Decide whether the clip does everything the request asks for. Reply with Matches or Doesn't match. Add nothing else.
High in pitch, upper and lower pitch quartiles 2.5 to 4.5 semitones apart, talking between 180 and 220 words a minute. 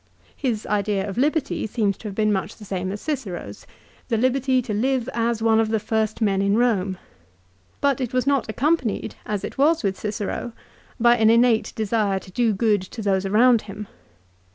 Matches